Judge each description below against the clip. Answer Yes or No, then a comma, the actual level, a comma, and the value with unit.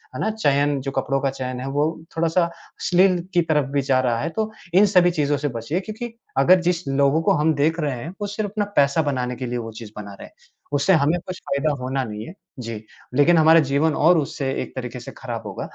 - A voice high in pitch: No, medium, 145 Hz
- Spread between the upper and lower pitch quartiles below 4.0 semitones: No, average, 4.8 semitones